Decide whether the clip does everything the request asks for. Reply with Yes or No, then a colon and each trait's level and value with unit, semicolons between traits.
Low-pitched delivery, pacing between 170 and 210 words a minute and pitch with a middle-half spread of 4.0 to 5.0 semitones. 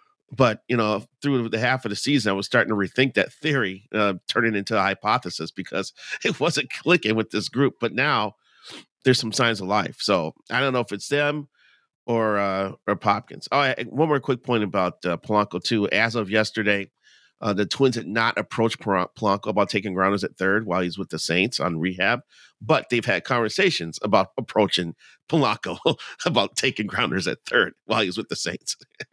Yes: low, 110 Hz; average, 195 wpm; average, 4.4 semitones